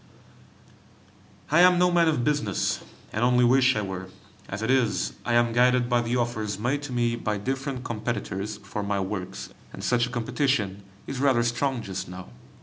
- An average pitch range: Yes, average, 3.9 semitones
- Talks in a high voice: No, low, 120 Hz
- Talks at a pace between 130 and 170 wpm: No, average, 180 wpm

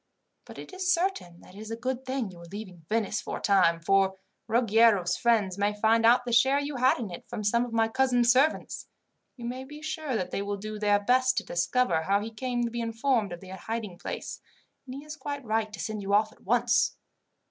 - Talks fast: Yes, fast, 235 wpm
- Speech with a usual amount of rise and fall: Yes, average, 4.0 semitones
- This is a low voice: No, high, 225 Hz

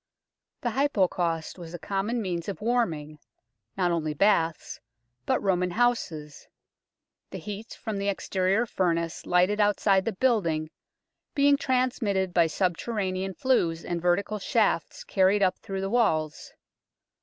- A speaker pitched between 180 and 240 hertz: Yes, high, 190 Hz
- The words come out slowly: Yes, slow, 130 wpm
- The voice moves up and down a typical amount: Yes, average, 4.0 semitones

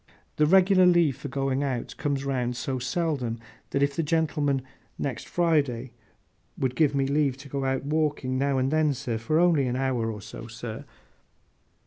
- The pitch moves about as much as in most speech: Yes, average, 3.1 semitones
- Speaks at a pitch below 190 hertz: Yes, medium, 140 Hz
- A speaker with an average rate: Yes, average, 165 wpm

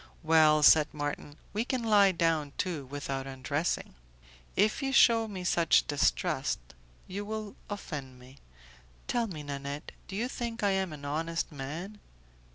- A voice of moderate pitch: Yes, medium, 165 Hz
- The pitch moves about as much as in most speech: No, wide, 6.1 semitones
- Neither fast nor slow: Yes, average, 150 wpm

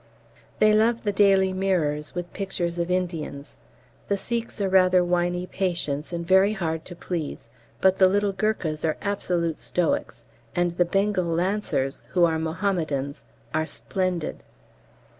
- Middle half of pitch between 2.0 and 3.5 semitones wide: Yes, average, 2.9 semitones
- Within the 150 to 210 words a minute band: No, average, 140 wpm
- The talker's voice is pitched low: No, medium, 180 Hz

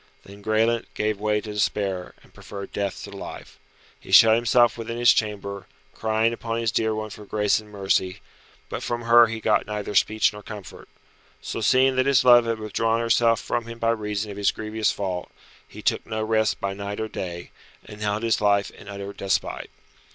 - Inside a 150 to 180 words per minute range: No, average, 195 wpm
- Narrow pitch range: Yes, narrow, 2.1 semitones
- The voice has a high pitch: No, low, 110 Hz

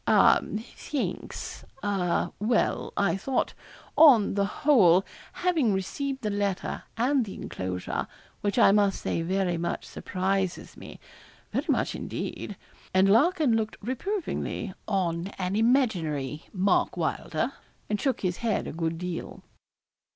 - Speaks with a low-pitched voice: No, high, 200 Hz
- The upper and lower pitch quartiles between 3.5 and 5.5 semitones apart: Yes, average, 4.9 semitones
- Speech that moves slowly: Yes, slow, 130 wpm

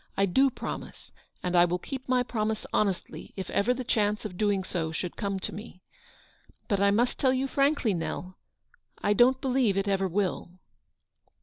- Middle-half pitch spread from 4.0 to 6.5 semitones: Yes, average, 4.9 semitones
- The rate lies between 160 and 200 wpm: Yes, average, 185 wpm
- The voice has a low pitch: No, high, 205 Hz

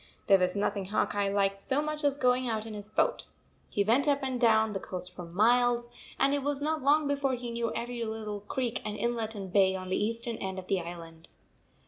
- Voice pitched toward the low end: No, high, 220 Hz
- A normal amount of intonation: Yes, average, 4.2 semitones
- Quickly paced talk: Yes, fast, 225 wpm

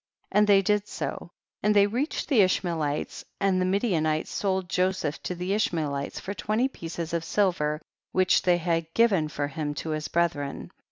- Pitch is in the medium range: Yes, medium, 180 Hz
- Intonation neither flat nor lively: Yes, average, 4.1 semitones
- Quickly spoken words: No, average, 190 wpm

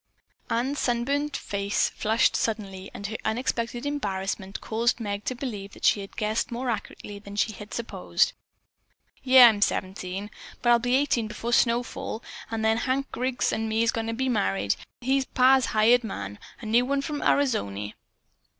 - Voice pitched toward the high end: Yes, high, 225 Hz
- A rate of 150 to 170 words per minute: Yes, average, 165 wpm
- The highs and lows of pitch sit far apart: No, average, 3.6 semitones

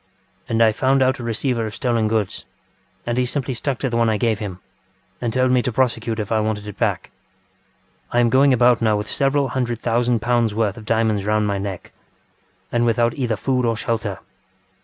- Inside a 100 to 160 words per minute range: No, fast, 205 wpm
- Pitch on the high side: No, low, 115 Hz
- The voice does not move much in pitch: Yes, narrow, 2.3 semitones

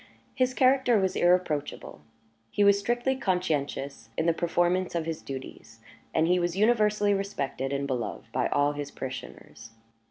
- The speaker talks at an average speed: Yes, average, 150 wpm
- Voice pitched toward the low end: No, medium, 175 Hz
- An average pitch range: No, wide, 6.3 semitones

